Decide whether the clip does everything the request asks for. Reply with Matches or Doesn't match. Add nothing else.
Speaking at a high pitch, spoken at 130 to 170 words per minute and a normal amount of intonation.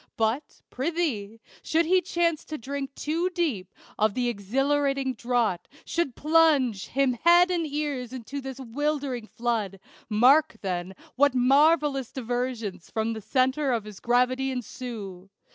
Matches